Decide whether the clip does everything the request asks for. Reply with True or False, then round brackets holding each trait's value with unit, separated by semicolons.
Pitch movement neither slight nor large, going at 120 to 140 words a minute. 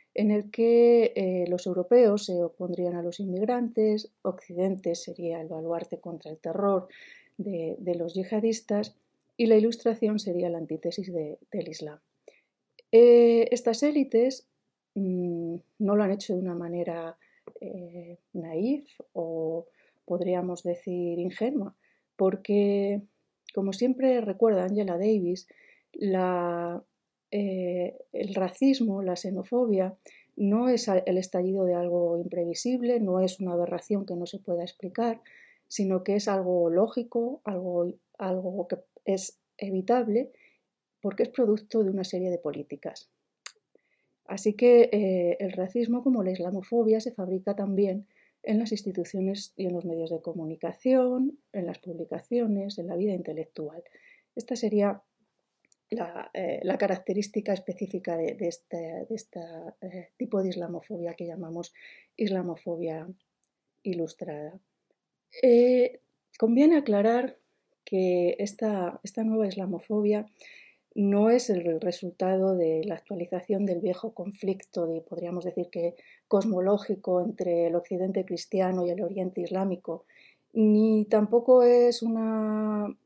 True (3.9 semitones; 130 wpm)